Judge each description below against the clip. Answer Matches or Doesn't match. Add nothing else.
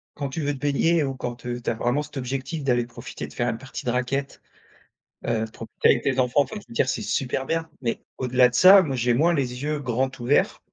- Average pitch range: Matches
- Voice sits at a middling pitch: Doesn't match